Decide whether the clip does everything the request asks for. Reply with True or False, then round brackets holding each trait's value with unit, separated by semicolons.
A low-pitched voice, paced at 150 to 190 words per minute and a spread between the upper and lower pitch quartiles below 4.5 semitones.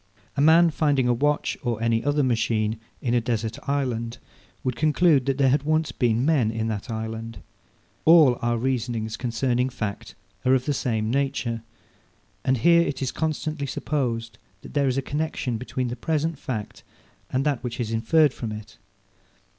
True (125 Hz; 170 wpm; 3.9 semitones)